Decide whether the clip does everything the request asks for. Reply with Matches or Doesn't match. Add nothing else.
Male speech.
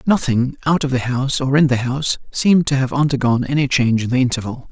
Matches